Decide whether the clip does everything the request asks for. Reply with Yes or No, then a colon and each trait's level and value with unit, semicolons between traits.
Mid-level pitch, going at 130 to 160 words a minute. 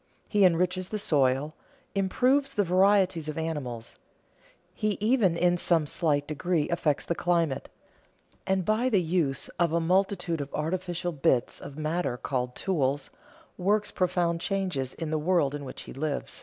Yes: medium, 170 Hz; average, 155 wpm